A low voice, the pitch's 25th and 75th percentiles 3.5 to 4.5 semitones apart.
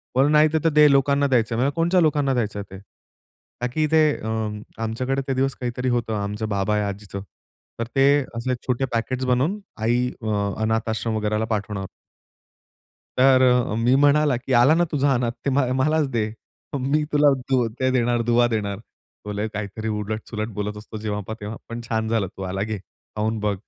Yes: low, 120 Hz; average, 4.0 semitones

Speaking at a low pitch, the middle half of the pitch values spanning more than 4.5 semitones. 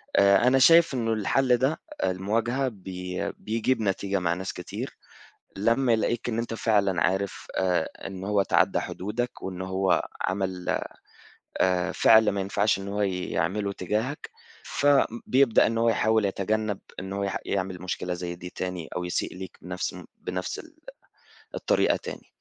No: low, 100 Hz; average, 3.6 semitones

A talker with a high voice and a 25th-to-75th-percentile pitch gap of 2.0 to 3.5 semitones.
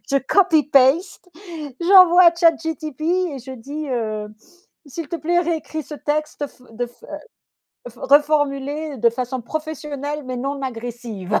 No: very high, 290 Hz; average, 3.9 semitones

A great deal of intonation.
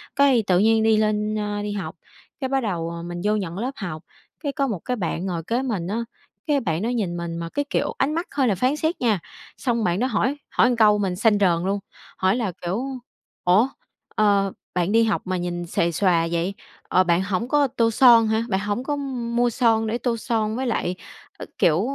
No: average, 4.9 semitones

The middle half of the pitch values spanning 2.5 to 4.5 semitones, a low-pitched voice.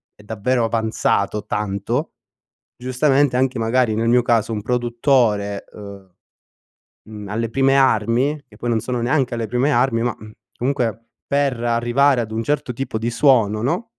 Yes: average, 2.9 semitones; low, 120 Hz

